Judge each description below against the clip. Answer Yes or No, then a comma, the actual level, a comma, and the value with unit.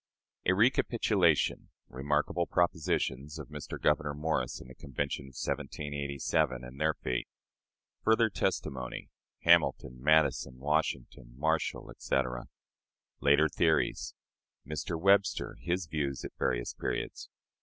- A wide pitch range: No, average, 3.6 semitones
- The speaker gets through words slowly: Yes, slow, 110 wpm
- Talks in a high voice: No, very low, 75 Hz